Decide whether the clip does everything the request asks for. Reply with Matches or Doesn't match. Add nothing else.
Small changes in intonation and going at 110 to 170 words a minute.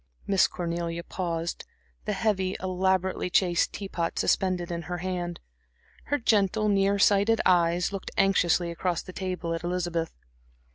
Matches